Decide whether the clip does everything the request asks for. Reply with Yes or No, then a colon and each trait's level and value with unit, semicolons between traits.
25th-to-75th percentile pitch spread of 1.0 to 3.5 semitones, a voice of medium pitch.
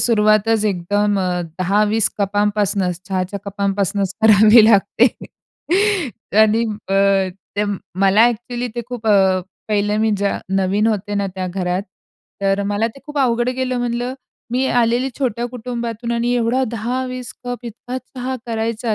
No: average, 3.1 semitones; high, 215 Hz